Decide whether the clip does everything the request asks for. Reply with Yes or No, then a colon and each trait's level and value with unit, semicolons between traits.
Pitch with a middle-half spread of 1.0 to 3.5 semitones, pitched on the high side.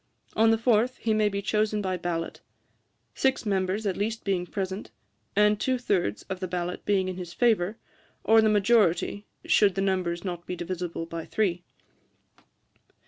Yes: average, 3.2 semitones; high, 195 Hz